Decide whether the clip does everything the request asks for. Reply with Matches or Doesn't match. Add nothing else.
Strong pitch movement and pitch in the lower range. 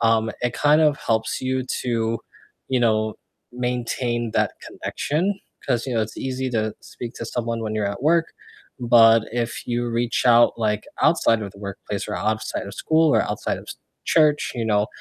Doesn't match